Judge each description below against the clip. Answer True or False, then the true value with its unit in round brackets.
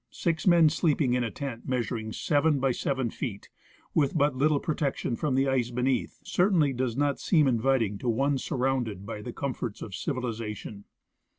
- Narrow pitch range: False (3.7 semitones)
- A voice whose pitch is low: True (130 Hz)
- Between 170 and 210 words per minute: True (175 wpm)